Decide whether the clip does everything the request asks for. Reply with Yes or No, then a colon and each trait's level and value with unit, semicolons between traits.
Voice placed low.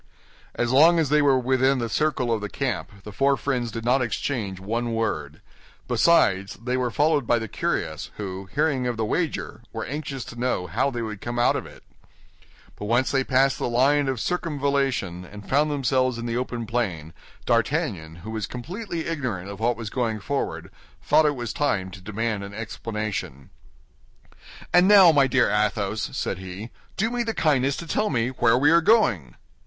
Yes: low, 120 Hz